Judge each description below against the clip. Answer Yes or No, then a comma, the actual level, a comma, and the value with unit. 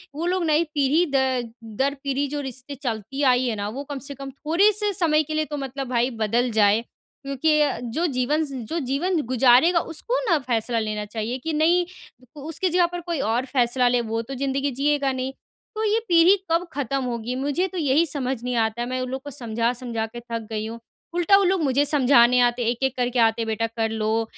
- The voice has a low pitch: No, very high, 265 Hz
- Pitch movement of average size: Yes, average, 4.2 semitones